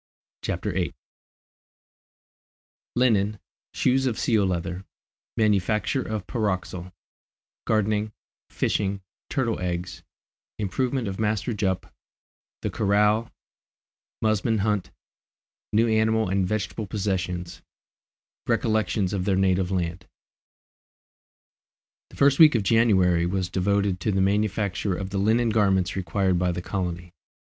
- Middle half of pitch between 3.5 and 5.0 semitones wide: No, average, 2.8 semitones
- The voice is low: Yes, low, 100 Hz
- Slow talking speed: Yes, slow, 110 wpm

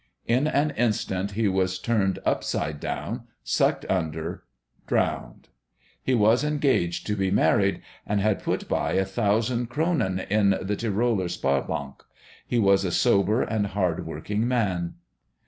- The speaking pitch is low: Yes, low, 100 Hz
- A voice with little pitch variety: No, average, 3.8 semitones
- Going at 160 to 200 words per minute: No, average, 140 wpm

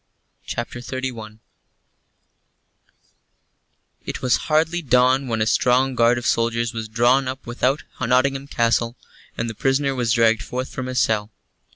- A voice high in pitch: No, low, 125 Hz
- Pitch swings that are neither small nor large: No, narrow, 2.2 semitones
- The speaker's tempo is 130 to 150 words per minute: Yes, average, 140 wpm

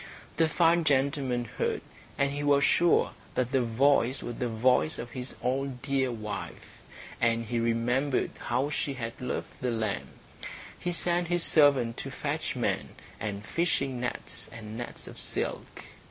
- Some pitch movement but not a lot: Yes, average, 3.6 semitones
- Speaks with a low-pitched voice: Yes, low, 130 Hz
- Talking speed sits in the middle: Yes, average, 155 wpm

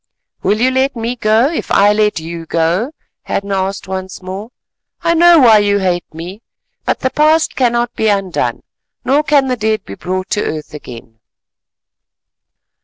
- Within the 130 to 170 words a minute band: Yes, average, 165 wpm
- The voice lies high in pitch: Yes, high, 210 Hz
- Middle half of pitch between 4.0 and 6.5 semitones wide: Yes, average, 5.2 semitones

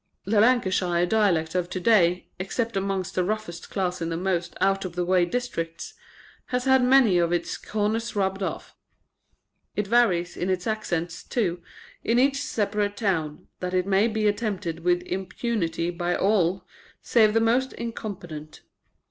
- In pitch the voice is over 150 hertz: Yes, high, 190 Hz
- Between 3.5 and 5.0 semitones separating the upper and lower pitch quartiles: Yes, average, 3.8 semitones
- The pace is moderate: Yes, average, 155 wpm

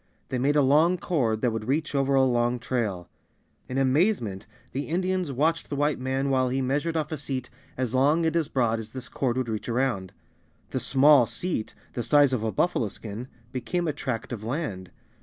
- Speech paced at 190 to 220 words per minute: Yes, average, 200 wpm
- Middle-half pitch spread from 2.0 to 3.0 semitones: No, average, 3.9 semitones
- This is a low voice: Yes, low, 130 Hz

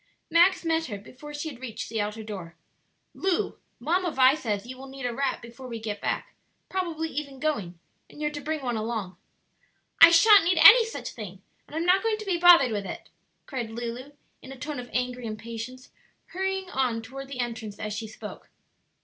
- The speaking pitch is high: Yes, very high, 260 Hz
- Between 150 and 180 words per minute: No, average, 200 wpm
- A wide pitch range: Yes, wide, 6.2 semitones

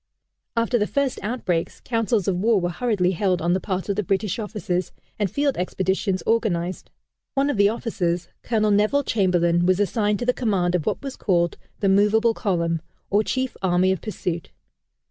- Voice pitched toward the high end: Yes, high, 200 Hz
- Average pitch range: Yes, average, 4.0 semitones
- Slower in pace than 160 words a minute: No, average, 180 wpm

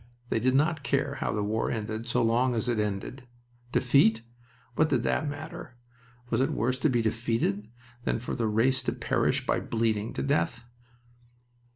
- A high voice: No, low, 120 Hz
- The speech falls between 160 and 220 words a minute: Yes, average, 175 wpm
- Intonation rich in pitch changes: No, average, 2.9 semitones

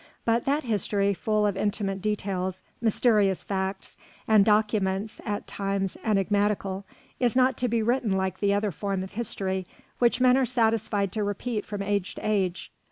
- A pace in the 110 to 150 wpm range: No, average, 165 wpm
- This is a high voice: Yes, high, 205 Hz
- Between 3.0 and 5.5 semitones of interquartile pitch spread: No, narrow, 2.4 semitones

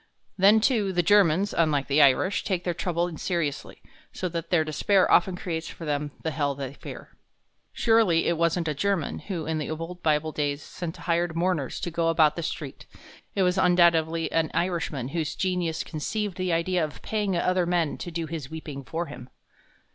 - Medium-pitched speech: Yes, medium, 165 Hz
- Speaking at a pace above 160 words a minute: Yes, average, 185 wpm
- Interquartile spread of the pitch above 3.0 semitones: No, average, 2.7 semitones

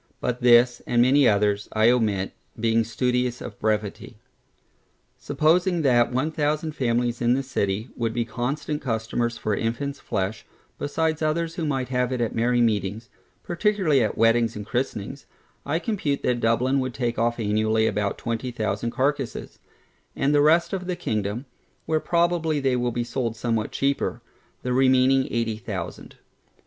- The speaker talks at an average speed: Yes, average, 160 wpm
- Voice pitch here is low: Yes, low, 125 Hz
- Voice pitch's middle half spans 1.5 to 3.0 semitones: No, average, 3.9 semitones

